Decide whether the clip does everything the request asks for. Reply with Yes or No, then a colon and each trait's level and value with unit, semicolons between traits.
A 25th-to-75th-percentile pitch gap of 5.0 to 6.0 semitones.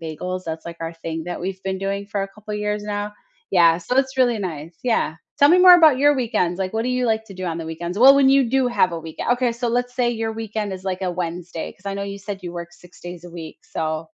Yes: wide, 5.6 semitones